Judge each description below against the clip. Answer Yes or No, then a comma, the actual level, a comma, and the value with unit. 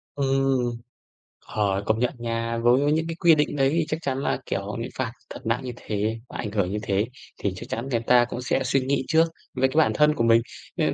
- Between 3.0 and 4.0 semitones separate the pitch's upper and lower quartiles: Yes, average, 3.5 semitones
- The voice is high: No, low, 125 Hz